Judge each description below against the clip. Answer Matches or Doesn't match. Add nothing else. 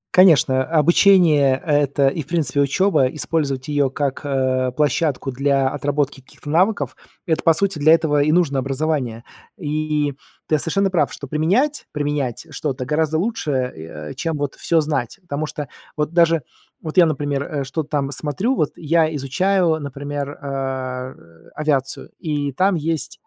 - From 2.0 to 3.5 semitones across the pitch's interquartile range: Matches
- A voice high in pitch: Doesn't match